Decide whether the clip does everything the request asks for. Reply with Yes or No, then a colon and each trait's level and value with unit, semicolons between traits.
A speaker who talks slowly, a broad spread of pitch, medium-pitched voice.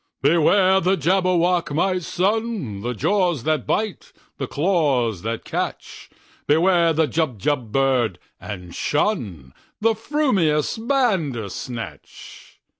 Yes: slow, 90 wpm; wide, 7.5 semitones; medium, 160 Hz